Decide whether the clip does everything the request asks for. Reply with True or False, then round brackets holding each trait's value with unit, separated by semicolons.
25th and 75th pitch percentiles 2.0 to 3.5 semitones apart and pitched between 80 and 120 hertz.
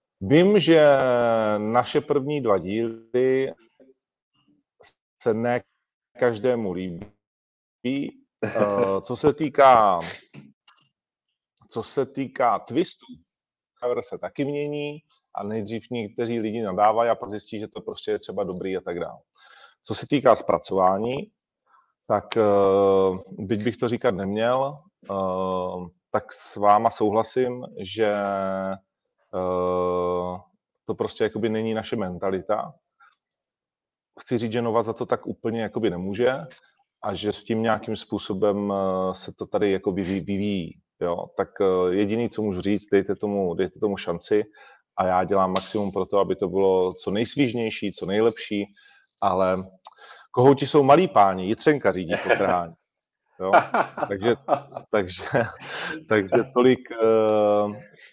False (4.2 semitones; 110 Hz)